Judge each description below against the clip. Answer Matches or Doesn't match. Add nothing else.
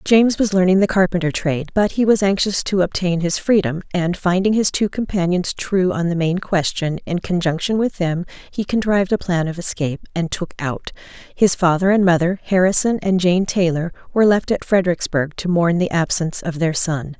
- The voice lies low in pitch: Doesn't match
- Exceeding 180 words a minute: Matches